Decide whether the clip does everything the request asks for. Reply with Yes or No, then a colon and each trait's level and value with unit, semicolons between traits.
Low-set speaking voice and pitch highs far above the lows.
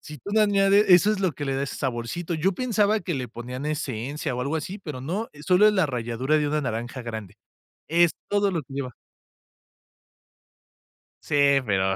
No: medium, 150 Hz; wide, 7.0 semitones